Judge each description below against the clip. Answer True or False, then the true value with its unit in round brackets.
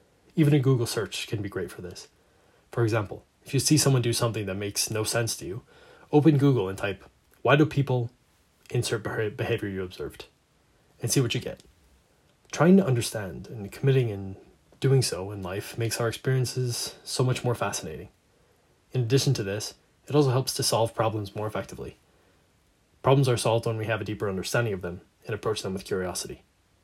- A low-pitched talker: True (115 Hz)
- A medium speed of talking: True (190 wpm)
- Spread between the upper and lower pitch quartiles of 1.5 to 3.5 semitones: False (4.6 semitones)